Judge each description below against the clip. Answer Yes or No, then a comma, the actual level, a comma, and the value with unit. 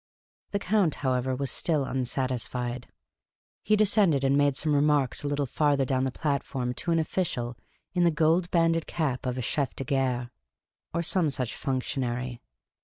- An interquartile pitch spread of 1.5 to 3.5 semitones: No, average, 4.0 semitones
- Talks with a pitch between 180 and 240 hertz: No, medium, 140 Hz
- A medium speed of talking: Yes, average, 165 wpm